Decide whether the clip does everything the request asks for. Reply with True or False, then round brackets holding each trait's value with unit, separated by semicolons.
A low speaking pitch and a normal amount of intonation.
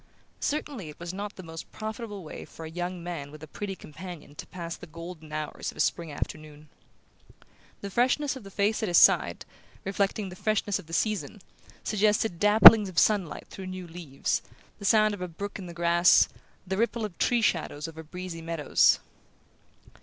False (180 Hz; 4.1 semitones)